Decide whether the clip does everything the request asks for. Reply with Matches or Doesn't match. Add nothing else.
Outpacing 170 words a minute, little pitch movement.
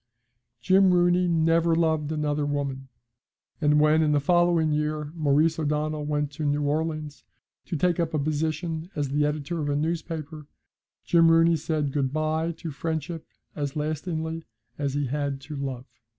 Doesn't match